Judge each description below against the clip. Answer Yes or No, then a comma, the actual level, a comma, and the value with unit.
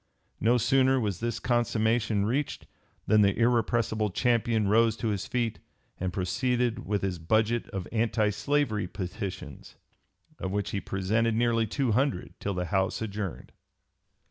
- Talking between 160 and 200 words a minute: No, average, 145 wpm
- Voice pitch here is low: Yes, low, 110 Hz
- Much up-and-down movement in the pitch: No, average, 3.0 semitones